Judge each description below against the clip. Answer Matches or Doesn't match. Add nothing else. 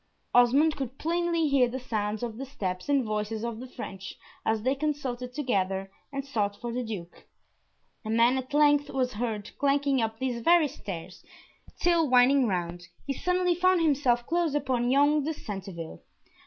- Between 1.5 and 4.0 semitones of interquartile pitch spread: Doesn't match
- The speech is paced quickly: Doesn't match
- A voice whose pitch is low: Doesn't match